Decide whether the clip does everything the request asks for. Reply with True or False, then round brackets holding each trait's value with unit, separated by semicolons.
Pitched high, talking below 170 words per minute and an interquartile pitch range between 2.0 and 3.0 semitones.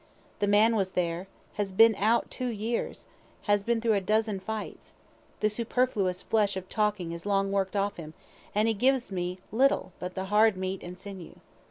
False (205 Hz; 185 wpm; 2.7 semitones)